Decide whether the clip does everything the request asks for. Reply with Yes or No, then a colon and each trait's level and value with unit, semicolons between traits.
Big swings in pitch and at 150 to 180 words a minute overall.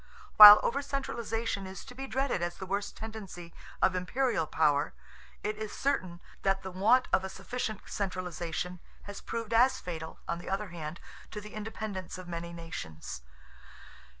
No: average, 4.2 semitones; average, 160 wpm